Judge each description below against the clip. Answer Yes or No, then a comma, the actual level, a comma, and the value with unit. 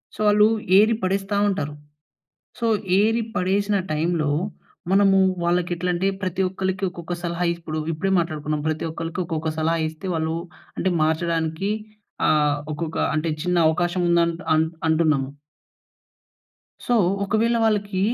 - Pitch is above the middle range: No, medium, 170 Hz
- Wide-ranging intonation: No, average, 3.3 semitones